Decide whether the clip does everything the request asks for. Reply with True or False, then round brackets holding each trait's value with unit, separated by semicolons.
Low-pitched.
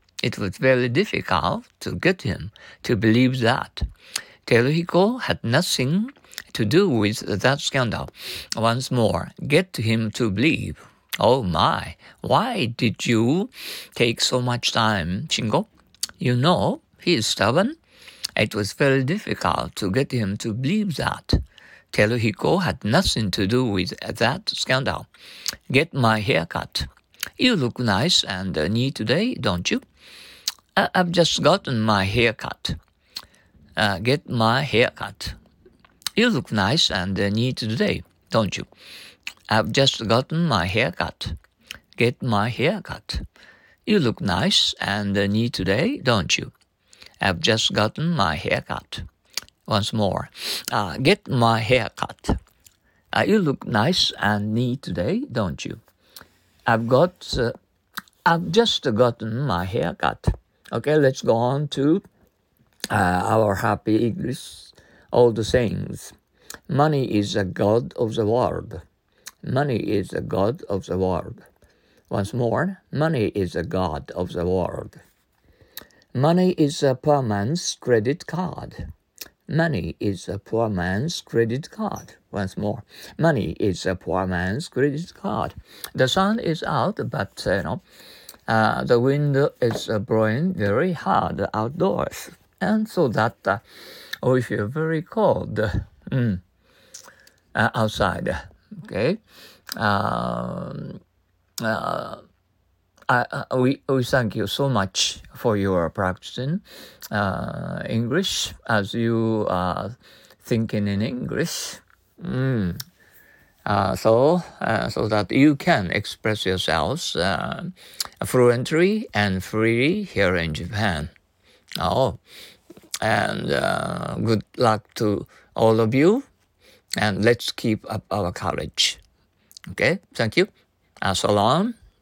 True (115 Hz)